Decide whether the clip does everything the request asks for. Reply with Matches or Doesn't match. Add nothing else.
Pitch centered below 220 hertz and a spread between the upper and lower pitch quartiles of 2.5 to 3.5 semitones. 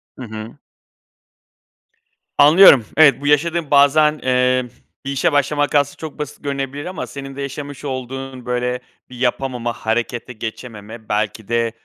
Matches